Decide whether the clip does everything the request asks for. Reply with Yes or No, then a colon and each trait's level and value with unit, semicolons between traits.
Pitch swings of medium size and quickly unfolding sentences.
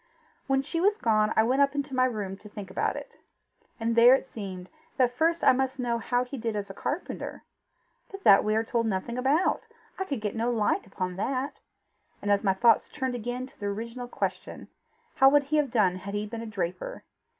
Yes: average, 4.2 semitones; fast, 215 wpm